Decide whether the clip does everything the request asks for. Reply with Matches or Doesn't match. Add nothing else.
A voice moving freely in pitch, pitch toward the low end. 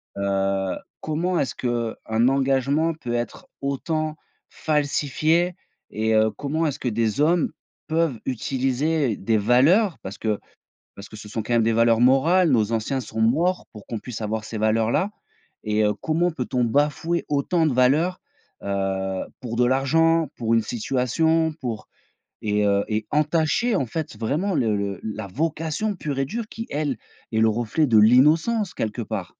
Matches